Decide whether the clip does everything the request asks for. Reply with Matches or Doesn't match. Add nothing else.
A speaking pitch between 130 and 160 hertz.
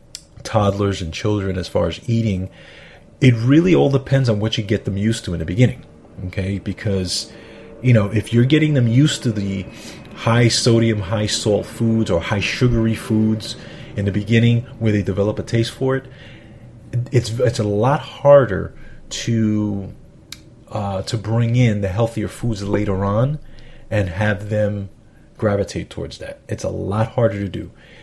Doesn't match